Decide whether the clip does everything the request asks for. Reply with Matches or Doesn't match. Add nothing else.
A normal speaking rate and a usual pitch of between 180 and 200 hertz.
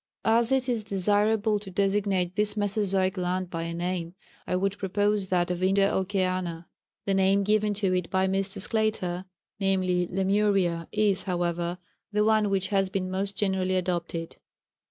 Matches